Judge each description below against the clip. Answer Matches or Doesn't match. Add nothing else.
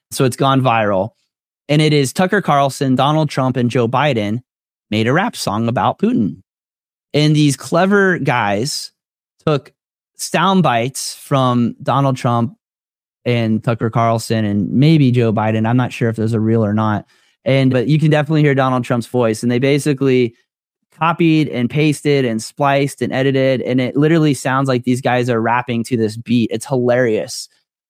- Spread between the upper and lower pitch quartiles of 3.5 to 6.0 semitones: Matches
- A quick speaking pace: Doesn't match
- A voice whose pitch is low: Matches